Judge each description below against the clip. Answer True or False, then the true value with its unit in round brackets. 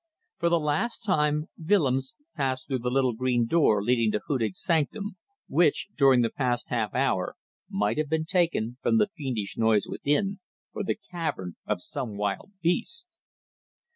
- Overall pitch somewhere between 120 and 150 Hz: True (135 Hz)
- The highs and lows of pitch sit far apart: True (6.4 semitones)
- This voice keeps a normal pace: True (160 wpm)